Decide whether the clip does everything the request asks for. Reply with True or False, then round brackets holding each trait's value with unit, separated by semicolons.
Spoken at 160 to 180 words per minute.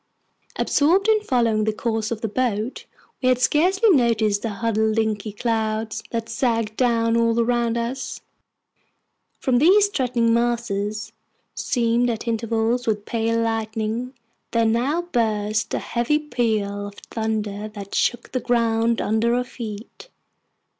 False (135 wpm)